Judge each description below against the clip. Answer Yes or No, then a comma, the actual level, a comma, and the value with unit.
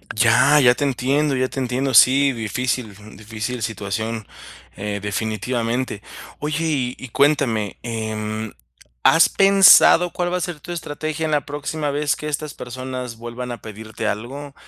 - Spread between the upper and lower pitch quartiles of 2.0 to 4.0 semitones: No, average, 4.7 semitones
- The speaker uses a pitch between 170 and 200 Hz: No, low, 125 Hz